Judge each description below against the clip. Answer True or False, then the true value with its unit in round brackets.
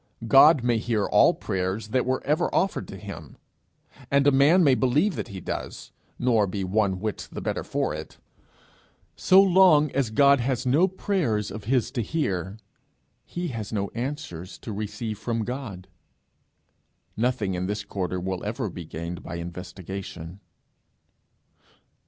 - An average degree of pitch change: False (6.4 semitones)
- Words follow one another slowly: False (150 wpm)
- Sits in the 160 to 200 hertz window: False (110 Hz)